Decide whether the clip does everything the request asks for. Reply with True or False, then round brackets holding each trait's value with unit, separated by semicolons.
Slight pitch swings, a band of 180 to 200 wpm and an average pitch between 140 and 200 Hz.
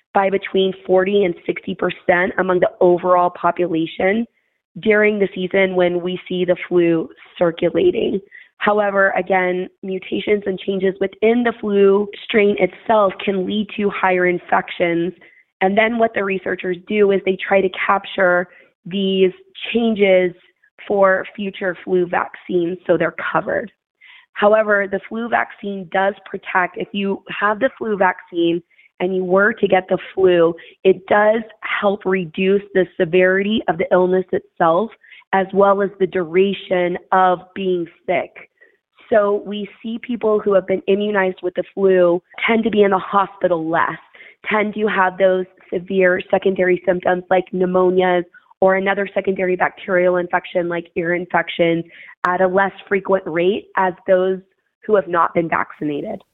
False (1.8 semitones; 145 wpm; 190 Hz)